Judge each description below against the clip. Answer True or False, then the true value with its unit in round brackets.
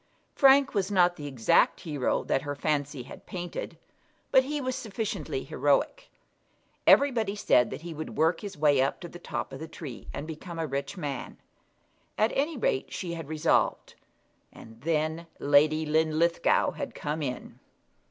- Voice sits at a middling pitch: True (160 Hz)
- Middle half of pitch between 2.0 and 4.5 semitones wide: False (4.9 semitones)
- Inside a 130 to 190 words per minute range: True (160 wpm)